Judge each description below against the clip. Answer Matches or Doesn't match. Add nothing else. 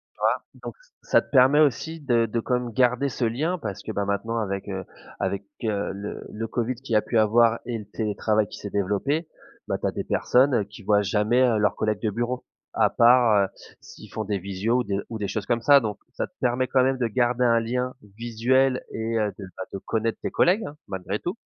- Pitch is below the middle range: Matches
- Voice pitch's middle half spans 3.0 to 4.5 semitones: Matches